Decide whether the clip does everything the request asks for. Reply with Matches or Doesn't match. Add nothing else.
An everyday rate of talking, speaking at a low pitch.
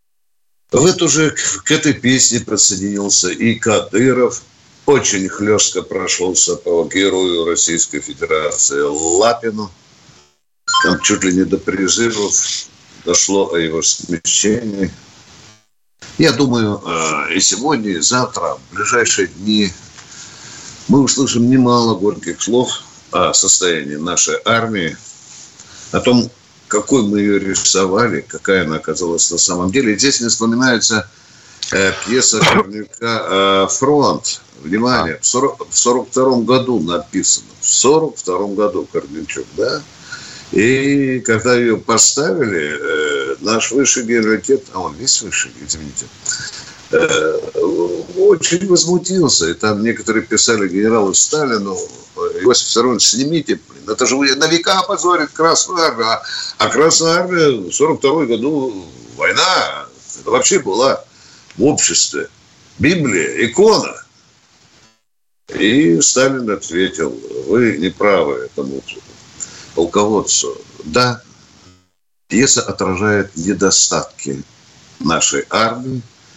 Doesn't match